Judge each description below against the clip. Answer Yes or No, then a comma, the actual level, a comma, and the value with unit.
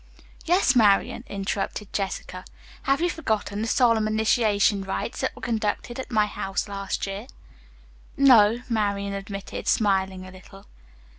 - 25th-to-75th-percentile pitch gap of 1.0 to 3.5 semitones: Yes, narrow, 2.6 semitones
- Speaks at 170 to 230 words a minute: No, slow, 135 wpm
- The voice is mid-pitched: No, high, 205 Hz